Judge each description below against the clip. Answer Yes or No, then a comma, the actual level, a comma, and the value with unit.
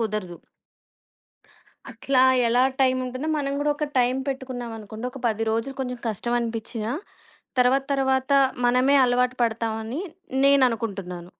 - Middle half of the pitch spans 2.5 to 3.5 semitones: Yes, average, 2.9 semitones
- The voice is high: Yes, high, 245 Hz